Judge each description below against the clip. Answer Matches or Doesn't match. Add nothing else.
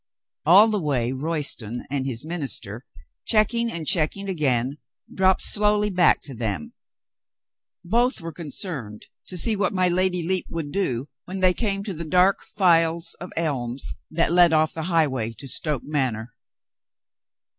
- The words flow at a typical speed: Matches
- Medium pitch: Matches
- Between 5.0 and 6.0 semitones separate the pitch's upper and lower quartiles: Matches